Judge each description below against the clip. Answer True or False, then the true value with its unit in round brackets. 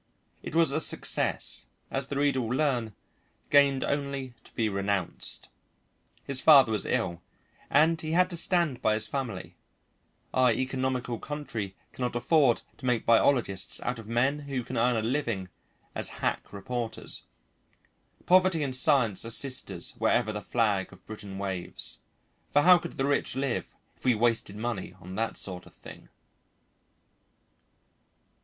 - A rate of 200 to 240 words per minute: False (150 wpm)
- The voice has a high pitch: False (125 Hz)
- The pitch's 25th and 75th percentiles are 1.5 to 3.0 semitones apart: False (4.4 semitones)